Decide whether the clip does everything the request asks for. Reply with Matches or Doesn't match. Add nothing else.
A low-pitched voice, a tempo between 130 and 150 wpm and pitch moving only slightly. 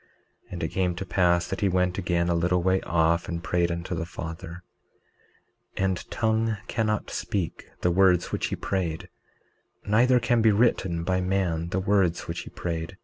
Doesn't match